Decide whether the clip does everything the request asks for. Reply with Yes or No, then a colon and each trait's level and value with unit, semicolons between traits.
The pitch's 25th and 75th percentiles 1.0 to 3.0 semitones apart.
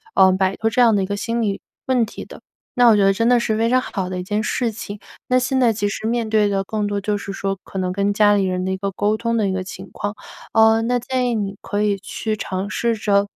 Yes: average, 2.7 semitones